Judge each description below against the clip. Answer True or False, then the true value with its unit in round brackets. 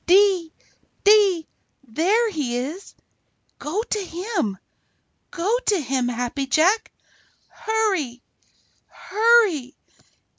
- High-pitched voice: True (350 Hz)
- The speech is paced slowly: True (90 wpm)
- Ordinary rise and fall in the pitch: False (7.5 semitones)